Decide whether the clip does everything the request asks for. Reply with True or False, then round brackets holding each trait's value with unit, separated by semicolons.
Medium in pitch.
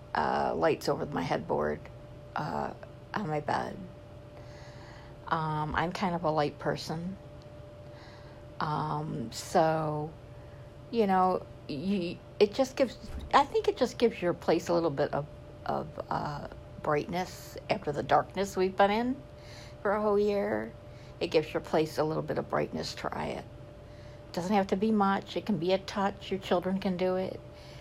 True (155 Hz)